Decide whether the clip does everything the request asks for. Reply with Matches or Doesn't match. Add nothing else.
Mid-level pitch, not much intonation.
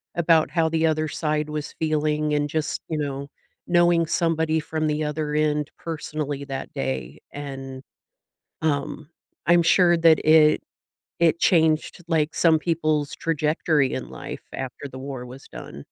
Matches